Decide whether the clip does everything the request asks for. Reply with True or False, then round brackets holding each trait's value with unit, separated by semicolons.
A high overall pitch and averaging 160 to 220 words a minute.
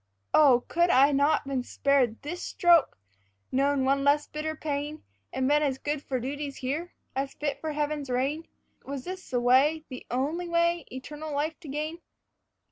True (290 Hz; 170 wpm)